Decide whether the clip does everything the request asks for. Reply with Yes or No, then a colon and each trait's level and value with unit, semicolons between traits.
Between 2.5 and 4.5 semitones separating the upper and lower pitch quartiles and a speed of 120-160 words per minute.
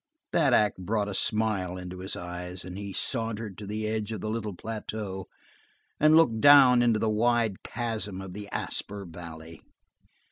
No: average, 3.4 semitones; average, 170 wpm